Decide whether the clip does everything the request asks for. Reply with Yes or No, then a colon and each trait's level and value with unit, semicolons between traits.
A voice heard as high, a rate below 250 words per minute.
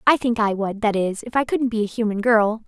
No: high, 220 Hz; fast, 270 wpm